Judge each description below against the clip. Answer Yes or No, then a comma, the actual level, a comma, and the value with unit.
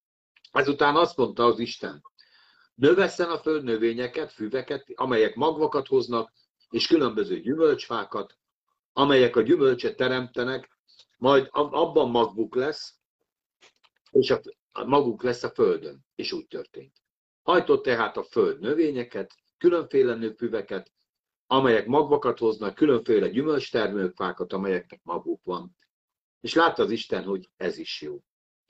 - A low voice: No, very high, 365 Hz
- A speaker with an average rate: Yes, average, 115 wpm